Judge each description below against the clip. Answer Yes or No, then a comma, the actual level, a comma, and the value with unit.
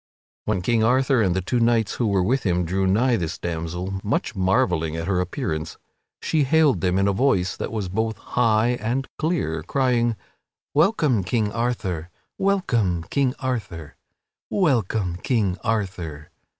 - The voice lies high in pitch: No, low, 105 Hz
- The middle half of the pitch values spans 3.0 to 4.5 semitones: No, wide, 5.5 semitones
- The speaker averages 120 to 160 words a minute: Yes, average, 150 wpm